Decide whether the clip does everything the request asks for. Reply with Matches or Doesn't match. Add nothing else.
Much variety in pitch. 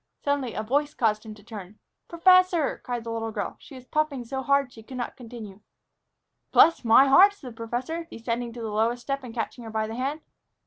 Doesn't match